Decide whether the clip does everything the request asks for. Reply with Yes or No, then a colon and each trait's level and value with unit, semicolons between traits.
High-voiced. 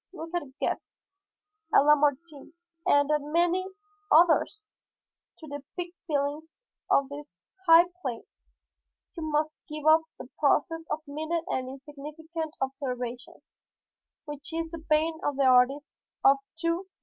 Yes: very high, 305 Hz